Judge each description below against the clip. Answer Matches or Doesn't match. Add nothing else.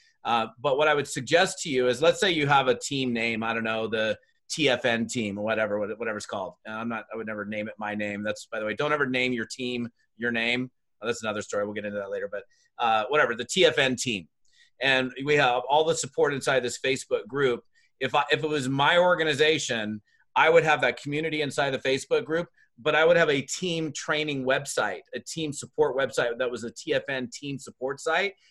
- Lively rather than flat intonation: Matches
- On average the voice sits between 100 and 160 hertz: Matches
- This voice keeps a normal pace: Doesn't match